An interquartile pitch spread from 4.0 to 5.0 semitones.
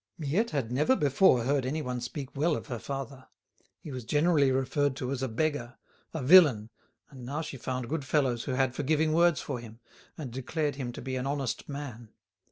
No: average, 2.9 semitones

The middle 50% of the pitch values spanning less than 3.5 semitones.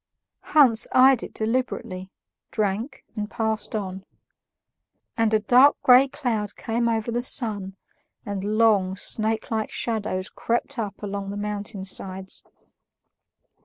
Yes: narrow, 2.6 semitones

